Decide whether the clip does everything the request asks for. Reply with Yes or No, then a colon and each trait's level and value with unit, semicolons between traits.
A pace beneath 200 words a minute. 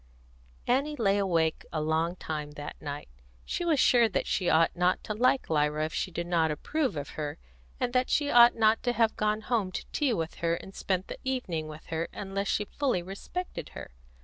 No: fast, 205 wpm